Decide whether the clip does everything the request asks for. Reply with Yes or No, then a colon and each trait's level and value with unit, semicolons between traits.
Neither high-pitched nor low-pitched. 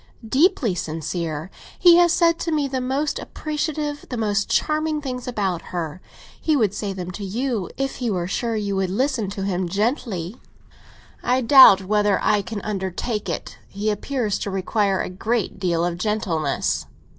No: high, 210 Hz